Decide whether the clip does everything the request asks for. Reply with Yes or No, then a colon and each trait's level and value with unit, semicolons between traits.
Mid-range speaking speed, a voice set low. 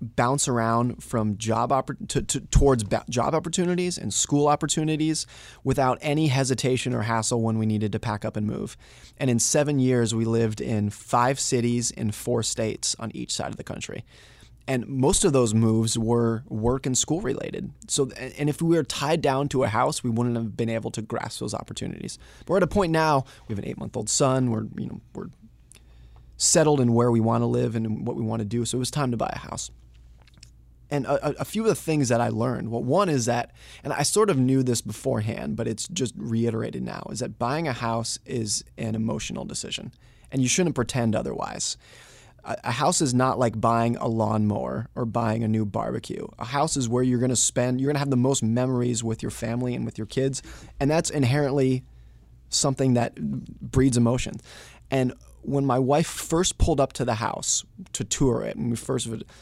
No: fast, 215 wpm; low, 120 Hz